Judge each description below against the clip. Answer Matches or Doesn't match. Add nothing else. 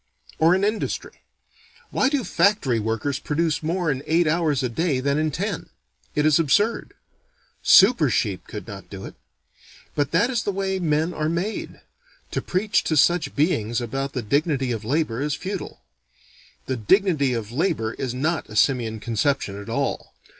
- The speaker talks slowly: Doesn't match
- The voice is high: Doesn't match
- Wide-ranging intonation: Matches